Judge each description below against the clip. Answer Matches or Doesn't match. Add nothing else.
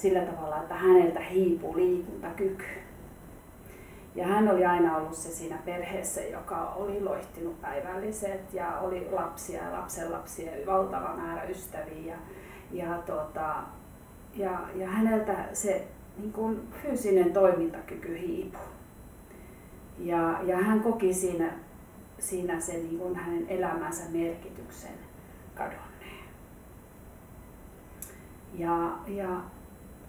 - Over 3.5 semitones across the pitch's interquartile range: Doesn't match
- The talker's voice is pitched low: Doesn't match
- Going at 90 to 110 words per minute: Matches